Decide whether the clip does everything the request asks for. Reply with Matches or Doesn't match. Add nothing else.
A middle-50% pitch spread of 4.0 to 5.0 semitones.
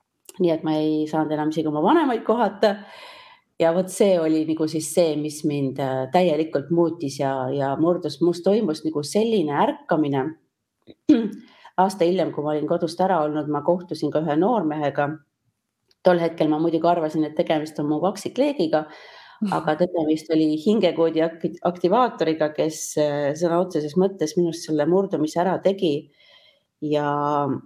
Doesn't match